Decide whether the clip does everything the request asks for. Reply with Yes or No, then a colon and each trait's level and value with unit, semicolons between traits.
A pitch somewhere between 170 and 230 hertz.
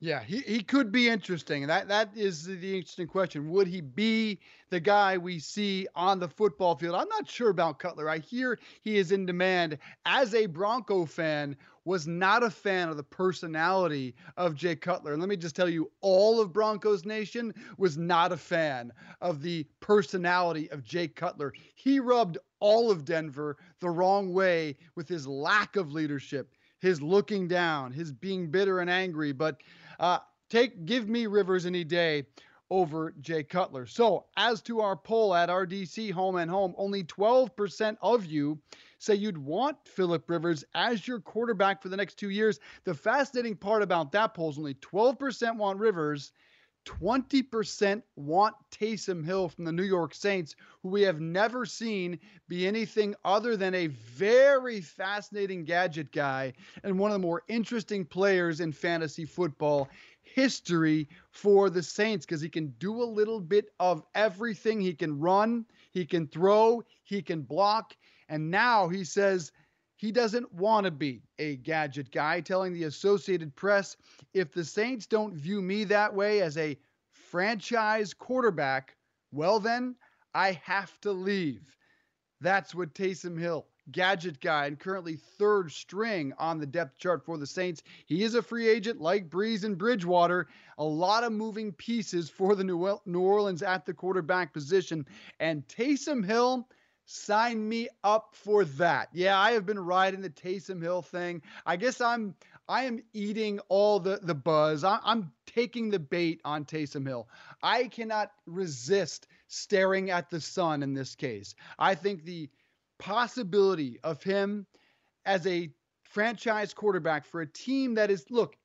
Yes: high, 190 Hz